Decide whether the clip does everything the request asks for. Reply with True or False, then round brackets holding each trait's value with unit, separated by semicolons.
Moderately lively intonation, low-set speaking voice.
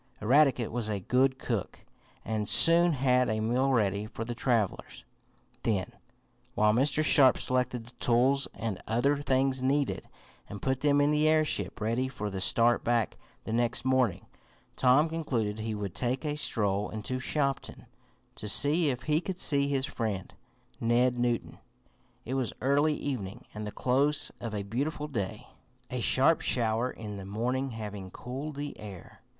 True (4.0 semitones; 125 Hz)